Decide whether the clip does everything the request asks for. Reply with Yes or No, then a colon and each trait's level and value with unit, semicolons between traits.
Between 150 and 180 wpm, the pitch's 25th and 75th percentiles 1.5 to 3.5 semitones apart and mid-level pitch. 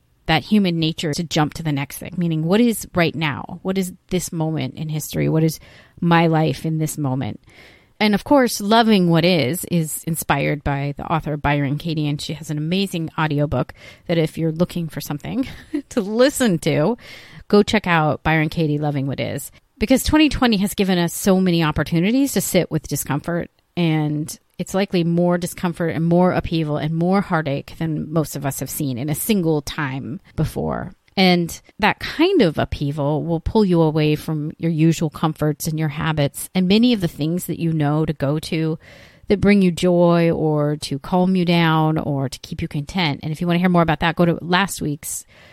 No: average, 200 wpm; average, 3.1 semitones; medium, 160 Hz